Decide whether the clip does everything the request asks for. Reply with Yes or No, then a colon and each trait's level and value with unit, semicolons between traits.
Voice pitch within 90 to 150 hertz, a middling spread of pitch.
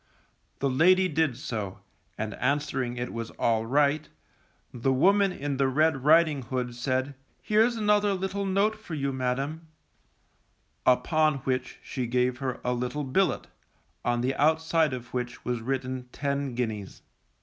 Yes: low, 135 Hz; average, 4.3 semitones